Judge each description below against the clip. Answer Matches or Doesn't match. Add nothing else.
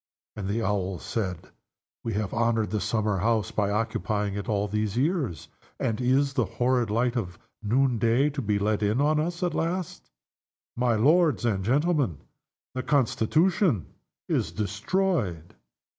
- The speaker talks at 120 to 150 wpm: Matches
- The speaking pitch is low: Matches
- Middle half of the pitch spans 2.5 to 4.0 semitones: Doesn't match